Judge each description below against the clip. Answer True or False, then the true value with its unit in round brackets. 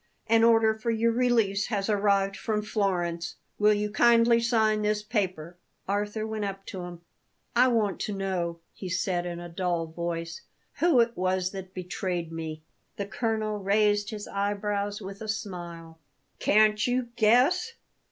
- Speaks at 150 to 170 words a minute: True (155 wpm)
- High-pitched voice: True (205 Hz)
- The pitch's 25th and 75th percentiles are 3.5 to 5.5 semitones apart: False (3.1 semitones)